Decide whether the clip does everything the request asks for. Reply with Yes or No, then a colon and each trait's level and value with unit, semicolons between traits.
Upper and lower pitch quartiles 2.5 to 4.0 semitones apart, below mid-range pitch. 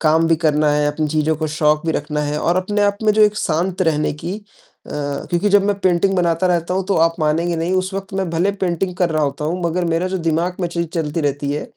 No: average, 3.2 semitones; medium, 170 Hz